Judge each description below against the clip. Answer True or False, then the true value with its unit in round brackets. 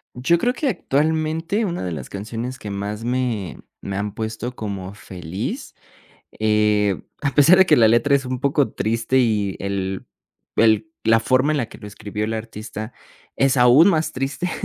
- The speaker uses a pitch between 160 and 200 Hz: False (115 Hz)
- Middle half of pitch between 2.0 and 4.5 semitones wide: False (5.2 semitones)